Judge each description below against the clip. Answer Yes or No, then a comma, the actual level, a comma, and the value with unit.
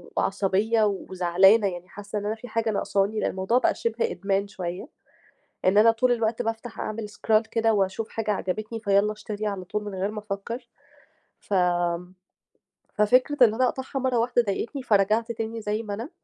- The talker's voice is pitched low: No, high, 215 Hz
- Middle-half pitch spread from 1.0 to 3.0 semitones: Yes, narrow, 2.5 semitones